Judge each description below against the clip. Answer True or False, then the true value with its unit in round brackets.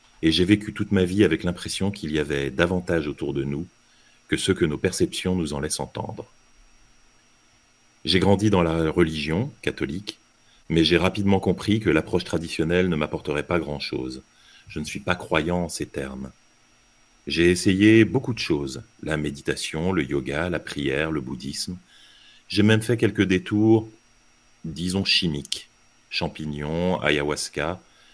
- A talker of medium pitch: False (85 Hz)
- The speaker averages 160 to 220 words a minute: False (150 wpm)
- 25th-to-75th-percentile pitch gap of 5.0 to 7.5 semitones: True (5.5 semitones)